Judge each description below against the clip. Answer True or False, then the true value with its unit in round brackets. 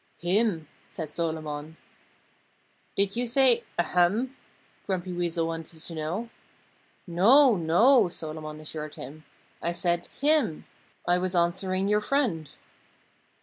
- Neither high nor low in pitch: True (175 Hz)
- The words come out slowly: True (110 wpm)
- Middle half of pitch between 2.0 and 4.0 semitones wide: False (4.6 semitones)